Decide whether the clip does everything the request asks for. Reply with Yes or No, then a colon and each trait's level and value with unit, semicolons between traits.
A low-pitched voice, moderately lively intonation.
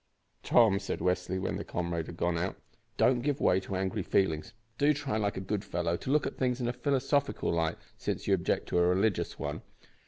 No: very low, 95 Hz; wide, 5.9 semitones